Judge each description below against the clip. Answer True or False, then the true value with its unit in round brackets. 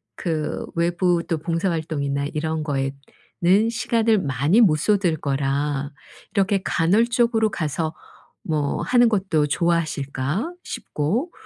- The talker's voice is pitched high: False (165 Hz)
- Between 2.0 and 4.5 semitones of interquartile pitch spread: False (5.4 semitones)